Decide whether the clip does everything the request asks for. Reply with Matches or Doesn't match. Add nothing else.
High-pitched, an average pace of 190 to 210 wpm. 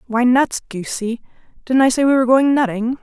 Matches